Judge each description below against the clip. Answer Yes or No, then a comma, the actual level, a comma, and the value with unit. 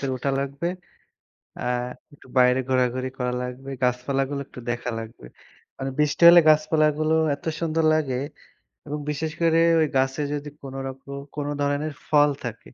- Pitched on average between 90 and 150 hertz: Yes, medium, 140 Hz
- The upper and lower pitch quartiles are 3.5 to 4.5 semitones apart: No, average, 2.8 semitones